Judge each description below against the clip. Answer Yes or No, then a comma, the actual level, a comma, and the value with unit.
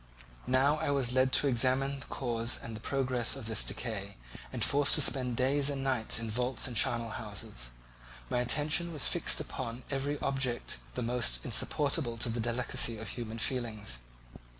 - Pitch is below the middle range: Yes, low, 125 Hz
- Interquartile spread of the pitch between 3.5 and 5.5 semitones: No, average, 2.9 semitones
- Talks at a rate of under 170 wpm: No, average, 175 wpm